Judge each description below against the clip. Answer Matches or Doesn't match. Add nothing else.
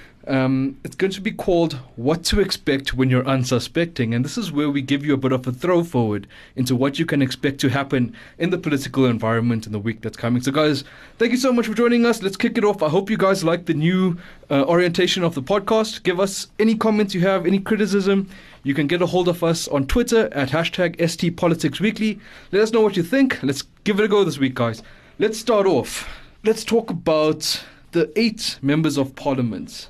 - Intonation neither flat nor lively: Doesn't match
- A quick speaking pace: Matches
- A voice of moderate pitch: Matches